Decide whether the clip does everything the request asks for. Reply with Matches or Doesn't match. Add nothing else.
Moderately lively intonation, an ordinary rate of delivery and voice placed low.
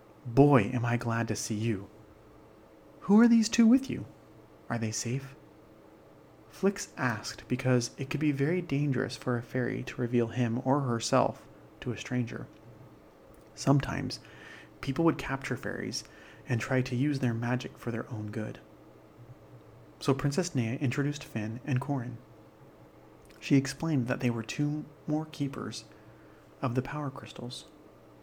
Matches